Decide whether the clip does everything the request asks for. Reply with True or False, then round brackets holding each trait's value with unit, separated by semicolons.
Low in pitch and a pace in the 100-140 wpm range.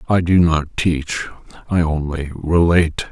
True (80 Hz; 135 wpm)